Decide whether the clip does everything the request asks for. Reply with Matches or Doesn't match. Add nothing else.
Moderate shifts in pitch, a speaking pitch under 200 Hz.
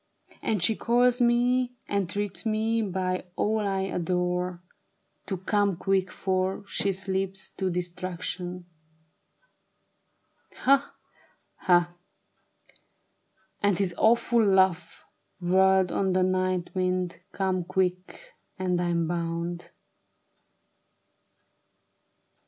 Doesn't match